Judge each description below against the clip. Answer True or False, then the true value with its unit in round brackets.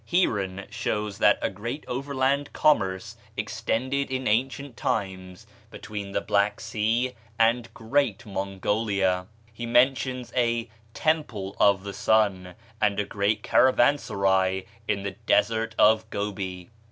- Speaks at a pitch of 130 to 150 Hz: False (110 Hz)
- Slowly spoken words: True (120 wpm)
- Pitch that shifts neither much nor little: True (4.0 semitones)